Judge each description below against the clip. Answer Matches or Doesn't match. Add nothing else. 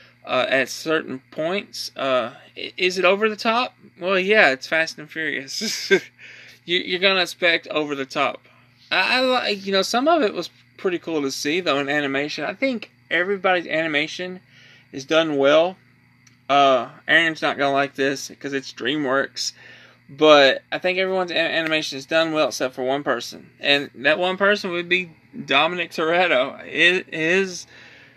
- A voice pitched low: Doesn't match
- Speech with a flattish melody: Doesn't match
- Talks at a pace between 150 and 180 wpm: Matches